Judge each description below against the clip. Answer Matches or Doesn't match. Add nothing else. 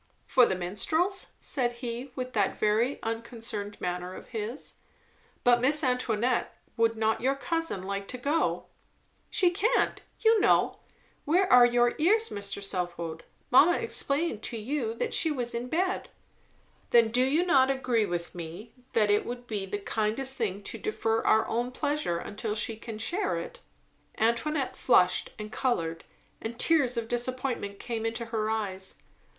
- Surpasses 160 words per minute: Doesn't match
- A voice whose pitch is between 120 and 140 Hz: Doesn't match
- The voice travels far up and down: Doesn't match